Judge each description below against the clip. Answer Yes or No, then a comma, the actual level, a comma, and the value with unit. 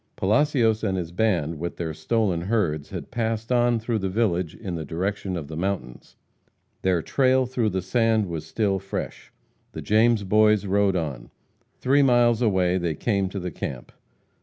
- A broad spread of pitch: No, average, 4.6 semitones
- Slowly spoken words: No, average, 170 wpm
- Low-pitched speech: Yes, low, 100 Hz